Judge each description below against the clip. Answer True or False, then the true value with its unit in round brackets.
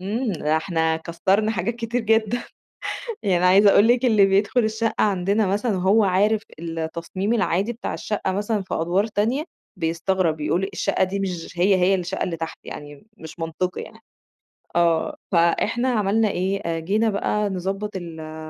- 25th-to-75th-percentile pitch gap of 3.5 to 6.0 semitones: True (3.8 semitones)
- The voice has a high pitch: True (195 Hz)